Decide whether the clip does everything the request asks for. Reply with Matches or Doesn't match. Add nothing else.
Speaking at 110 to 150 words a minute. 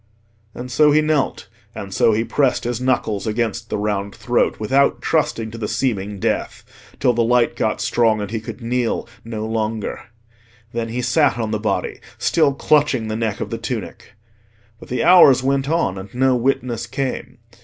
Doesn't match